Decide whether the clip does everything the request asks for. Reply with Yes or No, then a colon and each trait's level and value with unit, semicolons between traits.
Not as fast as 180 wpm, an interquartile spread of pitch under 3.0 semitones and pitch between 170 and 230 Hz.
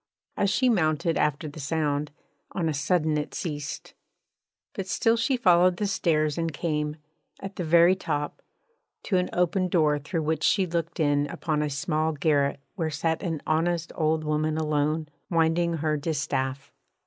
No: average, 160 wpm; narrow, 2.5 semitones; medium, 160 Hz